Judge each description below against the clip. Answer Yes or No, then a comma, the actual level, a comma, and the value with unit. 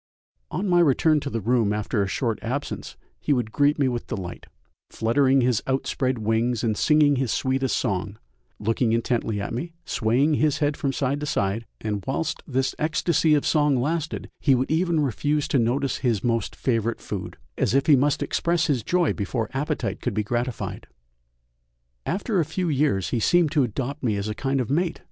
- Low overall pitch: Yes, low, 130 Hz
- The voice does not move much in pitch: No, average, 4.5 semitones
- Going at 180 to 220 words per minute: Yes, average, 190 wpm